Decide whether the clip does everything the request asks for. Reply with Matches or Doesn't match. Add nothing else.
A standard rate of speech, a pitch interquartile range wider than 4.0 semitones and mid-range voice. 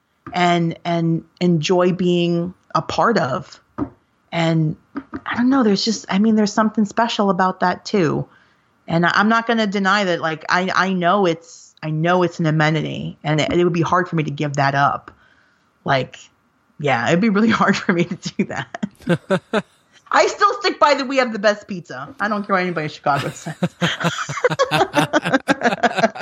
Matches